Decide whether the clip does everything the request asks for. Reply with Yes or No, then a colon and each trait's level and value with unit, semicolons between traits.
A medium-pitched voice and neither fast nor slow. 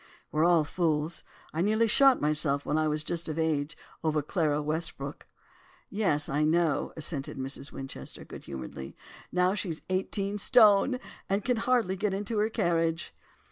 Yes: medium, 165 Hz; average, 155 wpm